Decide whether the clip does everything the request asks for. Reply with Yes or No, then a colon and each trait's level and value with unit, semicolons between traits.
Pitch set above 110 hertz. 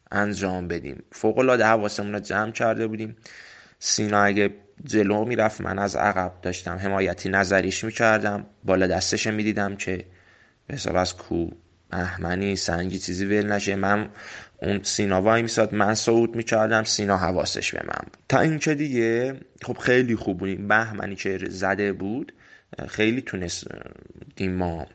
No: low, 100 Hz